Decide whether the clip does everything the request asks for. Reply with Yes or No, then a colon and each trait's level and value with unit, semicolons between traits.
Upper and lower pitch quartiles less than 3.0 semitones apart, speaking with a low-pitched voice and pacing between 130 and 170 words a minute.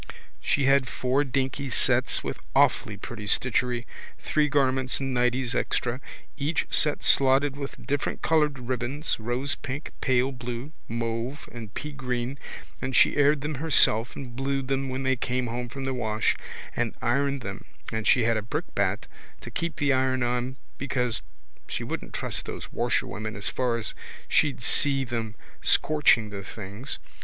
Yes: narrow, 2.6 semitones; low, 130 Hz; average, 155 wpm